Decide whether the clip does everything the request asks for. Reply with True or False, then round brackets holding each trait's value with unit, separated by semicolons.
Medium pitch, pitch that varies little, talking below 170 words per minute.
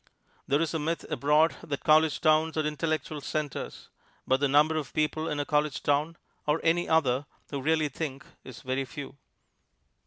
False (150 Hz; 1.9 semitones; 175 wpm)